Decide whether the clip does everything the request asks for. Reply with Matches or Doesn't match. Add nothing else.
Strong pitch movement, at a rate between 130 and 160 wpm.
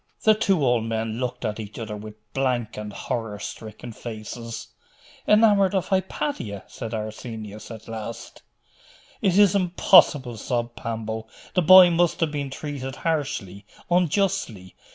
Matches